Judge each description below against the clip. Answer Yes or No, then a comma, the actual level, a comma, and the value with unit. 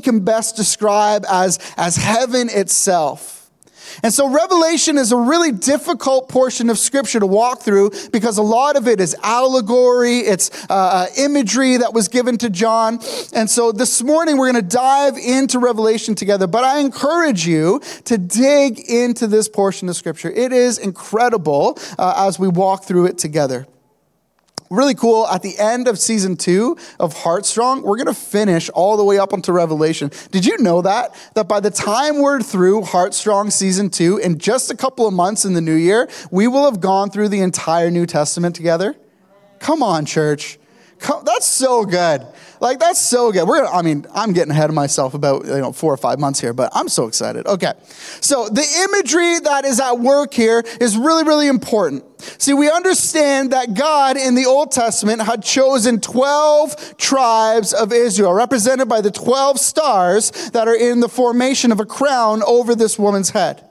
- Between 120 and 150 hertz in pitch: No, high, 225 Hz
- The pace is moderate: Yes, average, 185 wpm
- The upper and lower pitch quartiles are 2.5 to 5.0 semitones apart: No, wide, 5.5 semitones